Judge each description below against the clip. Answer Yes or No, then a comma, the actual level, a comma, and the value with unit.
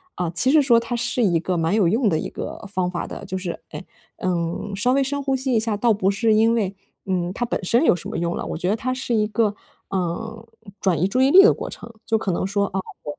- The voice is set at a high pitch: Yes, high, 210 Hz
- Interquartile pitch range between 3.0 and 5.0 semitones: Yes, average, 4.6 semitones